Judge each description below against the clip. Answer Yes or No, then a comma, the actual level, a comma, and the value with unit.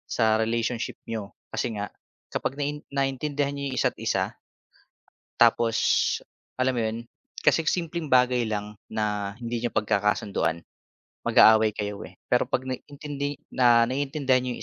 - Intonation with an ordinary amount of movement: Yes, average, 4.1 semitones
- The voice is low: Yes, low, 120 Hz